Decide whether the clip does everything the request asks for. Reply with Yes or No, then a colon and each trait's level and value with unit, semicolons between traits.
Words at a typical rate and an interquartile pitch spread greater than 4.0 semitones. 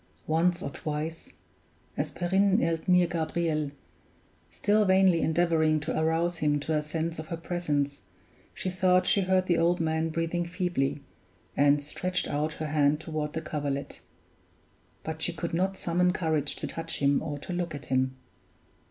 No: average, 160 wpm; average, 2.8 semitones